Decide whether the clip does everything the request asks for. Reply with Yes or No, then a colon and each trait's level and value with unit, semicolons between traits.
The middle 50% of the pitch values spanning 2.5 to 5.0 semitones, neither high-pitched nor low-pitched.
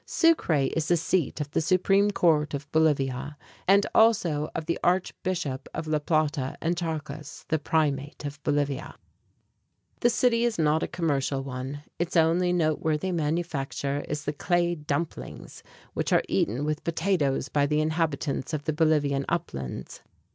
Yes: average, 3.1 semitones; medium, 155 Hz